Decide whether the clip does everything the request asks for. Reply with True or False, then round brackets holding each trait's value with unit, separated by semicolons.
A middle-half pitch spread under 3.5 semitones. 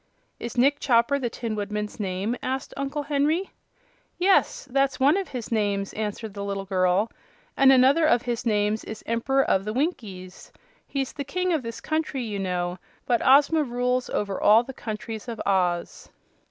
False (4.9 semitones)